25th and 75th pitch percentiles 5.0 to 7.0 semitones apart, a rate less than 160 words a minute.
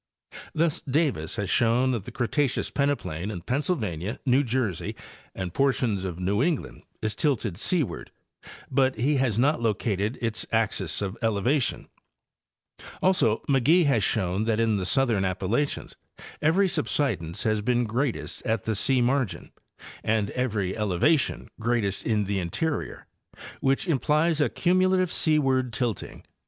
Yes: wide, 5.4 semitones; average, 140 wpm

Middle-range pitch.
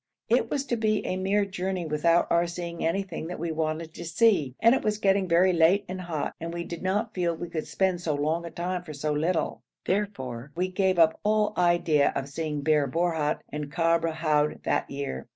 Yes: medium, 170 Hz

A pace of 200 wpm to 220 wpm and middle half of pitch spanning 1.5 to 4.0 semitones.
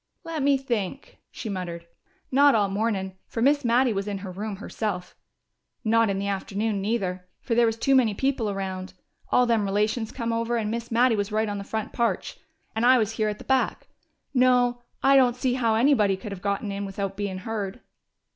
Yes: fast, 205 wpm; average, 3.5 semitones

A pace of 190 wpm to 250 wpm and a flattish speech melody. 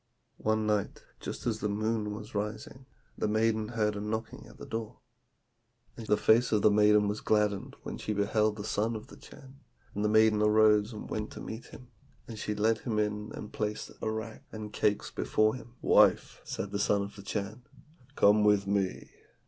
Yes: average, 195 wpm; narrow, 0.9 semitones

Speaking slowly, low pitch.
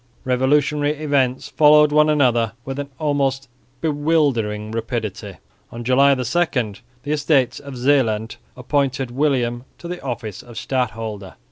Yes: slow, 120 wpm; low, 130 Hz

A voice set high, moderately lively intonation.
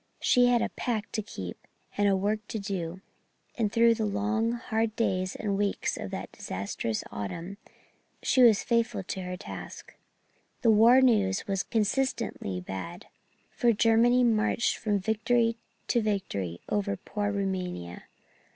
Yes: high, 210 Hz; average, 3.4 semitones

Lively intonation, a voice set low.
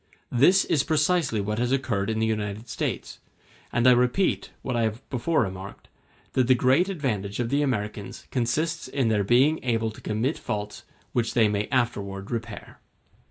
No: average, 4.0 semitones; low, 120 Hz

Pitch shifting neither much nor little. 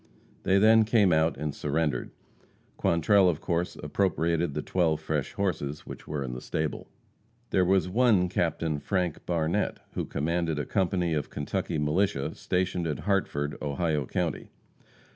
Yes: average, 3.6 semitones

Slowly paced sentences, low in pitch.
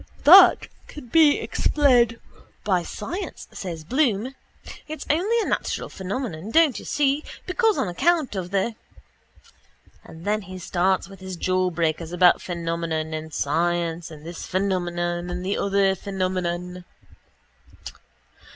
No: slow, 125 wpm; medium, 185 Hz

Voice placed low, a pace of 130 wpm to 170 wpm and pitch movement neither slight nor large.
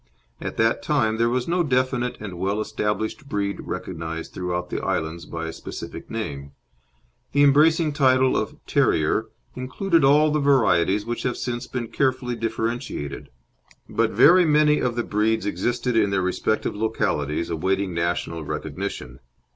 No: low, 115 Hz; average, 145 wpm; wide, 6.3 semitones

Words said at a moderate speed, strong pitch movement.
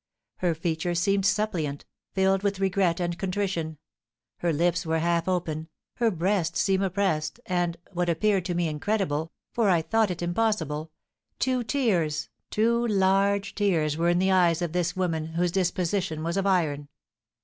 No: average, 160 wpm; average, 3.1 semitones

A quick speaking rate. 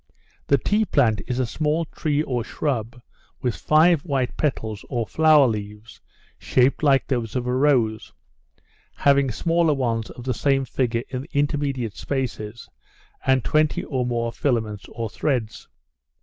No: average, 150 wpm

